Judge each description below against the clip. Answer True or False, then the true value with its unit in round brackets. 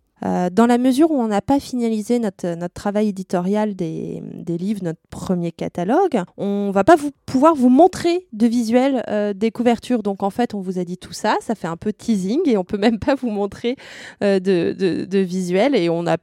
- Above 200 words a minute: True (220 wpm)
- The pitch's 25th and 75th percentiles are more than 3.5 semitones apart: True (4.4 semitones)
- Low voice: False (210 Hz)